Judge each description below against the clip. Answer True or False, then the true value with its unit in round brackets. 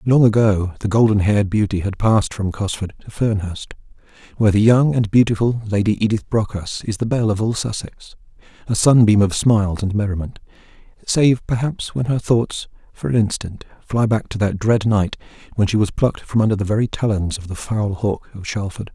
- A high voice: False (105 Hz)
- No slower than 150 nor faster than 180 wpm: False (195 wpm)